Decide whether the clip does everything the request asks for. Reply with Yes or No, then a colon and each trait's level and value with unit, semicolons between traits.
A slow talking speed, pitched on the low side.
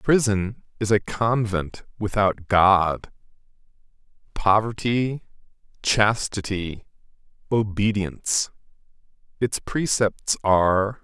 Yes: slow, 70 wpm; low, 105 Hz